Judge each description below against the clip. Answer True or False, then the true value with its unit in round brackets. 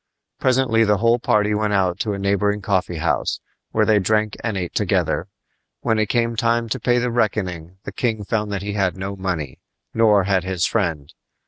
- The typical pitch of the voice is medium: False (105 Hz)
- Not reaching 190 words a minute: False (195 wpm)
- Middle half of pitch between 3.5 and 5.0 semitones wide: False (3.1 semitones)